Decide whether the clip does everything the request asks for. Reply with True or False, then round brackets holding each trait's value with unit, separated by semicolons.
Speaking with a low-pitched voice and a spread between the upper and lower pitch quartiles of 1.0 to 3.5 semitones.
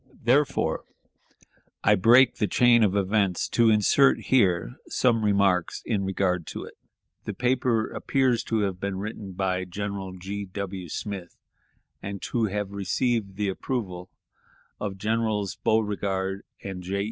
True (100 Hz; 2.8 semitones)